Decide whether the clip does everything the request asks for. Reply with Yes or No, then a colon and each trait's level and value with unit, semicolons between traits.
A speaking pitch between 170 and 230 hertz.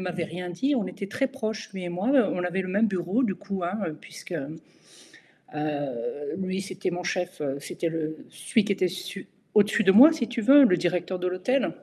Yes: medium, 185 Hz